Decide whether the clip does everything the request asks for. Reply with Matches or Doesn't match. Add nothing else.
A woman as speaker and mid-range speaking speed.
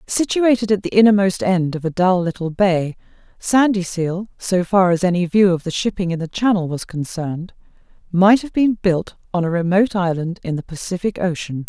Matches